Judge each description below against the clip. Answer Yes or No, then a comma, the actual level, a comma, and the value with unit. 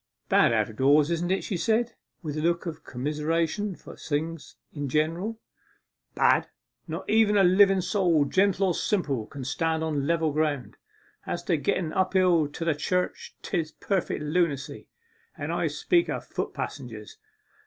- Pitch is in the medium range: Yes, medium, 165 Hz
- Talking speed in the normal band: Yes, average, 165 wpm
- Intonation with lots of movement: No, average, 4.0 semitones